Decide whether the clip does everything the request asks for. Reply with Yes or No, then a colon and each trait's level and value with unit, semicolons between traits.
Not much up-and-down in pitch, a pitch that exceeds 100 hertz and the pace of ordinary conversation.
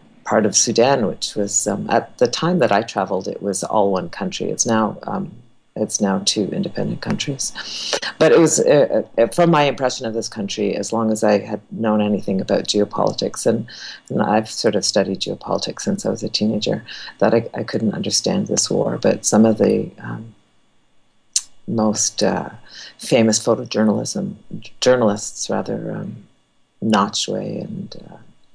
Yes: narrow, 1.5 semitones; low, 110 Hz; average, 165 wpm